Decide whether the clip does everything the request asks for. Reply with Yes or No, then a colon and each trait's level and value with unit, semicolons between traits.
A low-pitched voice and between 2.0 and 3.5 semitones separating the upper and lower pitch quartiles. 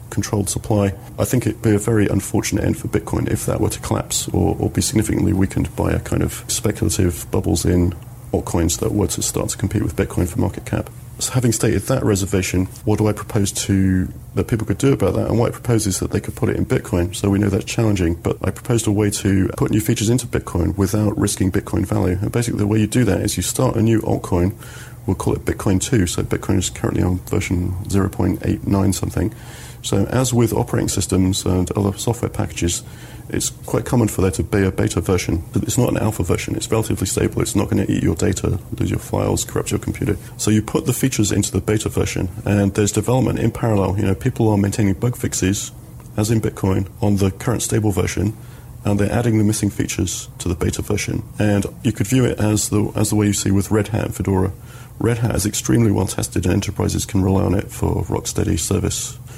Yes: low, 105 Hz; average, 2.7 semitones